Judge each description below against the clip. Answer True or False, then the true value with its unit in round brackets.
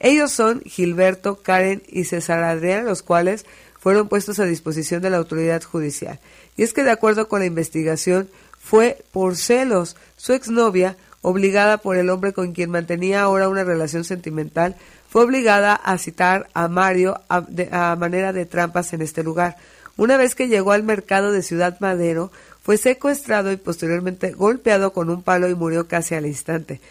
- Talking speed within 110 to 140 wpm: False (175 wpm)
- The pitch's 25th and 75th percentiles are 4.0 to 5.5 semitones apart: False (3.0 semitones)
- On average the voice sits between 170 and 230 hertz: True (185 Hz)